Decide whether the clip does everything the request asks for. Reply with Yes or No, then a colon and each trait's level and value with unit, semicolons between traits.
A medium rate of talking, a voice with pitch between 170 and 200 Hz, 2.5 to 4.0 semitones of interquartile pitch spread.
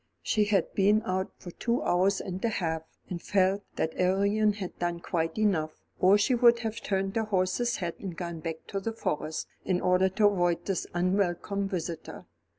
Yes: average, 185 wpm; high, 190 Hz; average, 2.8 semitones